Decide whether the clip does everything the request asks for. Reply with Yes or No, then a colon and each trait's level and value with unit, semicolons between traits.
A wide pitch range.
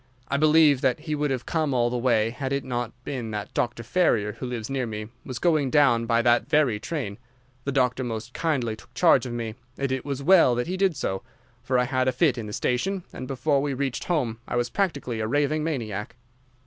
No: average, 3.8 semitones